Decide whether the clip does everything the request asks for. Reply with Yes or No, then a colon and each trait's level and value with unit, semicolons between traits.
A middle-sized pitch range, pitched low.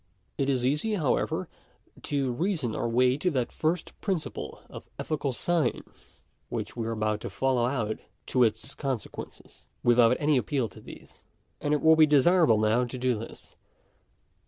Yes: average, 4.2 semitones; low, 130 Hz